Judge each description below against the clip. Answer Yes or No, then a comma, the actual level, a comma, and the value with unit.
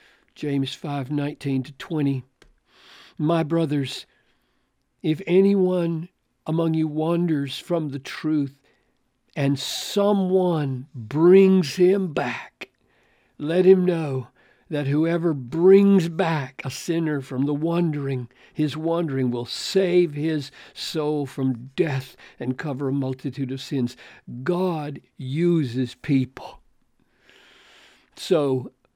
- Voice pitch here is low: No, medium, 150 Hz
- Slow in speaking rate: Yes, slow, 105 wpm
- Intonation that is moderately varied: Yes, average, 4.1 semitones